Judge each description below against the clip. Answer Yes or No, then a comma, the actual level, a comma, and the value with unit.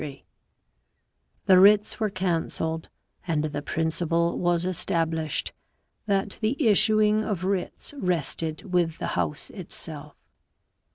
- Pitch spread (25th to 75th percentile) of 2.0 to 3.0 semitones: No, average, 3.7 semitones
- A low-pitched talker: No, medium, 175 Hz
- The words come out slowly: Yes, slow, 120 wpm